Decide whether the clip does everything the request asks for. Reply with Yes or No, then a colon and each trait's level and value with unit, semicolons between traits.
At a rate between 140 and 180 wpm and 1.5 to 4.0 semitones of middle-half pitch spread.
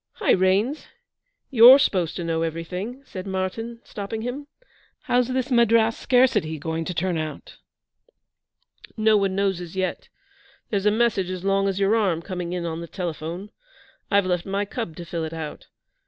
No: average, 170 wpm; average, 4.5 semitones